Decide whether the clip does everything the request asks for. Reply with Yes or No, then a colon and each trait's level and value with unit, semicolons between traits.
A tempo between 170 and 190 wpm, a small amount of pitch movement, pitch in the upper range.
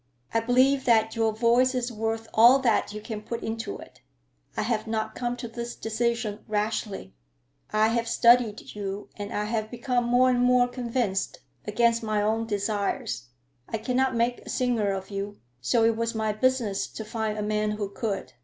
Yes: average, 180 wpm; narrow, 2.2 semitones; high, 225 Hz